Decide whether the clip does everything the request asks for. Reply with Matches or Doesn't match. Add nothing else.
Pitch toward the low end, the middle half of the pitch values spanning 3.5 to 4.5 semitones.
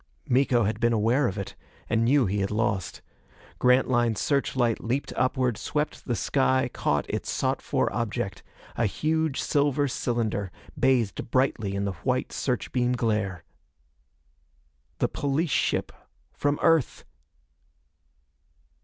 Matches